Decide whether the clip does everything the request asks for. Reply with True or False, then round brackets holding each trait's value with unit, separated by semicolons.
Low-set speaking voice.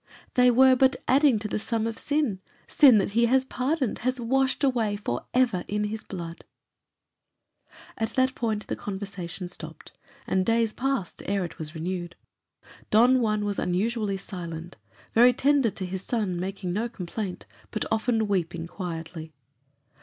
False (215 Hz)